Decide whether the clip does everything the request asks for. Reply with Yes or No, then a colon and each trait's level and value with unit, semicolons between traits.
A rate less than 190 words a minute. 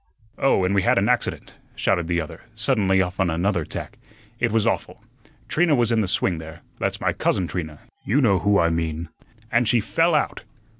No: average, 200 wpm